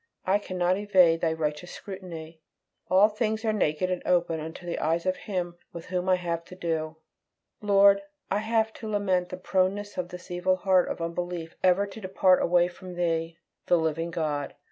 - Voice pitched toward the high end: No, medium, 180 Hz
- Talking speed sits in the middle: Yes, average, 185 wpm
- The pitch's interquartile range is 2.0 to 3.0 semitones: Yes, narrow, 2.5 semitones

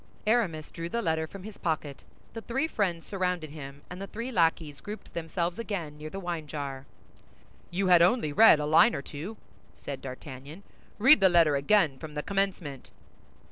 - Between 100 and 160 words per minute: No, average, 180 wpm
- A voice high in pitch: No, medium, 170 Hz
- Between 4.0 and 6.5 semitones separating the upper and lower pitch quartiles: Yes, average, 4.9 semitones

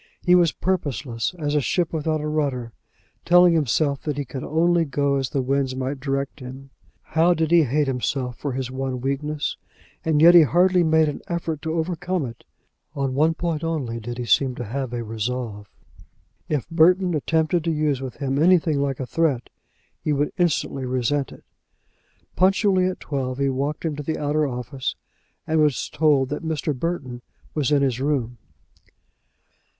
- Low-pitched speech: No, medium, 145 Hz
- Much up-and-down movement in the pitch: No, average, 3.5 semitones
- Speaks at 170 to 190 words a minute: Yes, average, 175 wpm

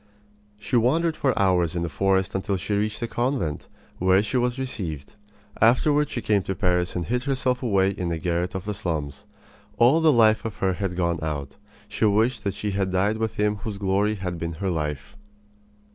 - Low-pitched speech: Yes, low, 100 Hz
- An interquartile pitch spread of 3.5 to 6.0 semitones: Yes, average, 4.3 semitones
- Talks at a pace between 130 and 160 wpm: No, fast, 205 wpm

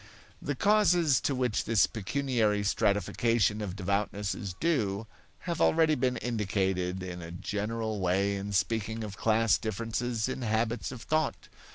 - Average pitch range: Yes, average, 3.7 semitones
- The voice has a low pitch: Yes, low, 110 Hz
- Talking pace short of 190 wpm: Yes, average, 145 wpm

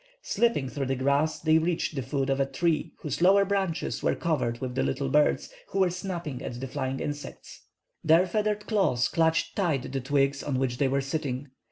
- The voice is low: No, medium, 145 Hz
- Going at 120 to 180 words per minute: No, average, 200 wpm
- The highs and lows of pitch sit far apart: No, average, 4.2 semitones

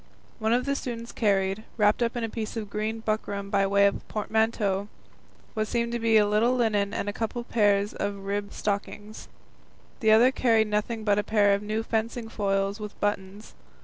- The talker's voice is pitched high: Yes, high, 215 Hz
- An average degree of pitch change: No, narrow, 1.9 semitones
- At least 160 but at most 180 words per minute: No, average, 200 wpm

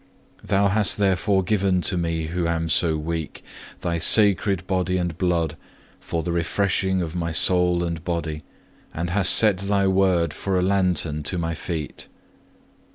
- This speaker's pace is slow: No, average, 160 wpm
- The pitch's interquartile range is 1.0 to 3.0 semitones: Yes, narrow, 2.5 semitones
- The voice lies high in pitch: No, very low, 90 Hz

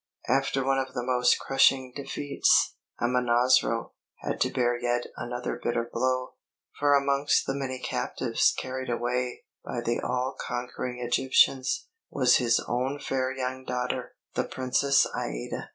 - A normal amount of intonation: No, narrow, 1.6 semitones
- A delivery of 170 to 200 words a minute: No, slow, 135 wpm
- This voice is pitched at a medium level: No, low, 125 Hz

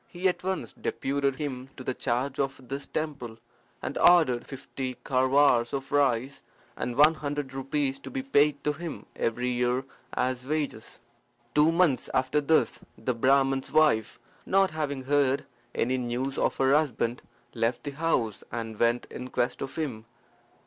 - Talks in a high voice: No, low, 135 Hz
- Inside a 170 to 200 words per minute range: No, average, 155 wpm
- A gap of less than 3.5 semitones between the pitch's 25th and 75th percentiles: Yes, average, 2.9 semitones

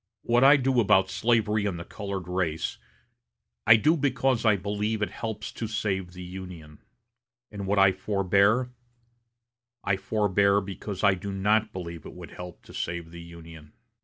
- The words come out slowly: No, average, 165 wpm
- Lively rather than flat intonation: No, average, 3.2 semitones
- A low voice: Yes, low, 100 Hz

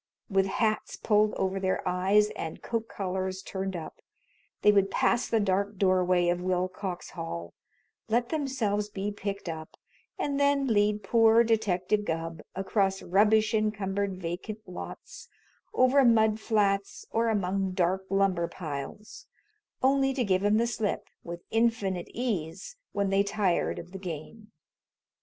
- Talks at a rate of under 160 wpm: Yes, average, 140 wpm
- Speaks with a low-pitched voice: No, high, 200 Hz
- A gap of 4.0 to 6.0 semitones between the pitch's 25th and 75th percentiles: No, average, 2.9 semitones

